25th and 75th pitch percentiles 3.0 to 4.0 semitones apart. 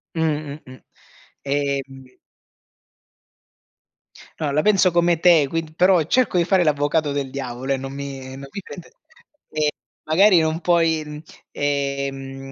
Yes: average, 3.3 semitones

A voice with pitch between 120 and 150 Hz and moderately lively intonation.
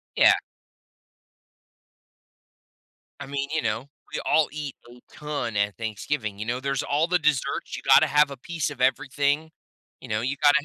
Yes: medium, 140 Hz; average, 3.6 semitones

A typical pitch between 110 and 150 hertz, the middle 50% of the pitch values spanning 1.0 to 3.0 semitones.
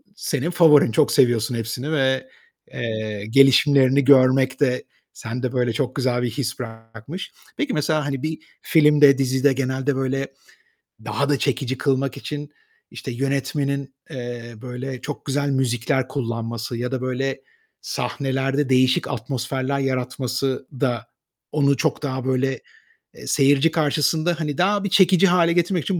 Yes: low, 135 Hz; narrow, 2.5 semitones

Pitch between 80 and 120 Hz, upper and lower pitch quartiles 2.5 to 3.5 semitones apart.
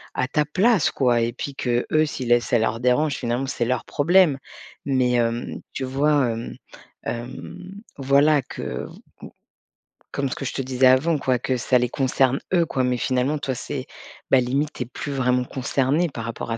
No: low, 130 Hz; average, 2.8 semitones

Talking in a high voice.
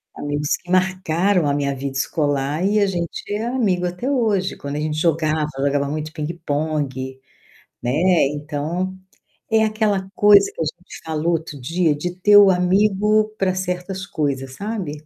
No: medium, 170 Hz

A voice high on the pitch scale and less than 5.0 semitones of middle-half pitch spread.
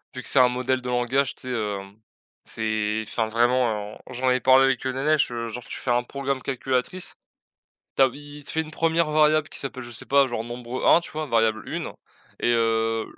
No: low, 125 Hz; average, 2.9 semitones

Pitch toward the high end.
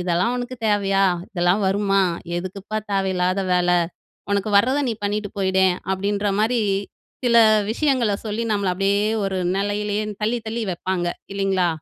Yes: high, 200 Hz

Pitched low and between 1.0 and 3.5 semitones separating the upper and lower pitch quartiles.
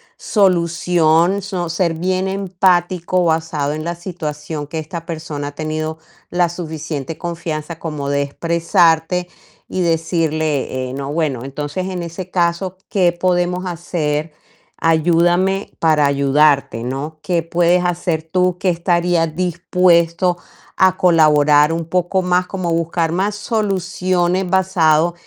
No: medium, 170 Hz; narrow, 2.4 semitones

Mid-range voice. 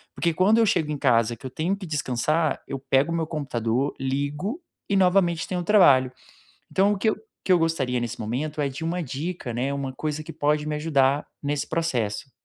Yes: medium, 150 Hz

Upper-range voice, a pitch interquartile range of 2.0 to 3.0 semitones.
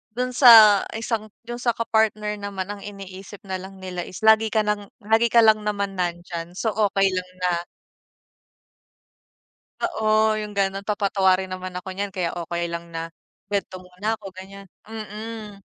Yes: high, 200 Hz; narrow, 2.6 semitones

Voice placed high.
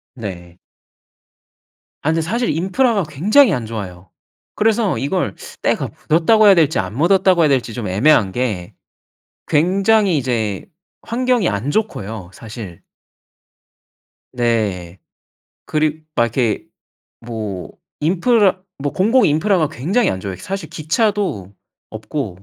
No: medium, 150 Hz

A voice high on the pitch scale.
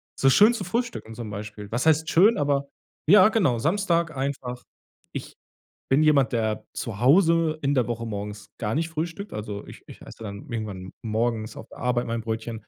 No: low, 125 Hz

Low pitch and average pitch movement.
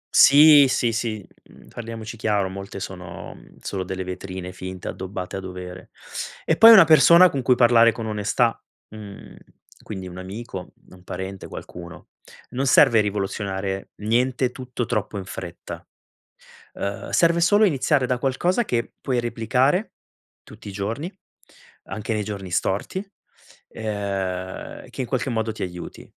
Yes: low, 110 Hz; average, 4.9 semitones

